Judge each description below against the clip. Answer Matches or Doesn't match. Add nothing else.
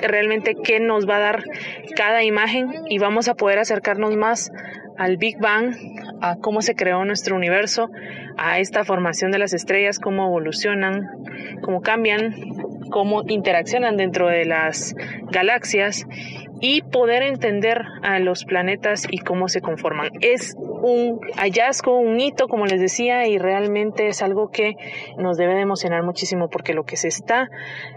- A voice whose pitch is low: Doesn't match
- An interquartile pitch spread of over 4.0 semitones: Doesn't match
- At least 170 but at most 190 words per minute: Doesn't match